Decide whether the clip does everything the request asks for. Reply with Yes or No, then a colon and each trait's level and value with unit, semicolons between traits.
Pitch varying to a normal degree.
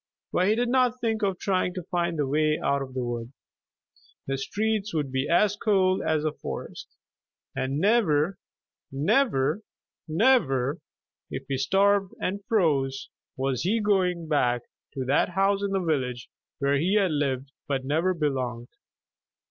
No: wide, 6.6 semitones